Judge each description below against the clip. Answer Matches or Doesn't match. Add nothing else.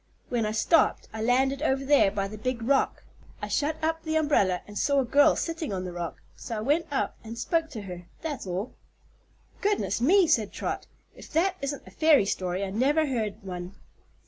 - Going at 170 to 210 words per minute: Matches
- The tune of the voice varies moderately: Doesn't match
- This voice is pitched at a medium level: Doesn't match